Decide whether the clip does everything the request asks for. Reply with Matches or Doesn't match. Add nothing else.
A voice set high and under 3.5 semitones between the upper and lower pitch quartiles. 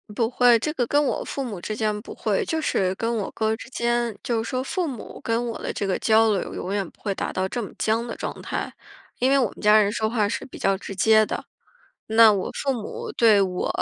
Matches